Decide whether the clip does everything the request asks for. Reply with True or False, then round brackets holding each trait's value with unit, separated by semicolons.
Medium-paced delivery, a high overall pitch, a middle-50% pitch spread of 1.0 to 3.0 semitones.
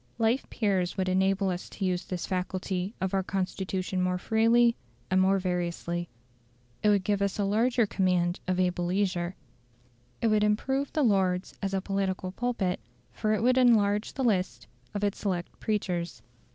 True (165 wpm; 195 Hz; 2.6 semitones)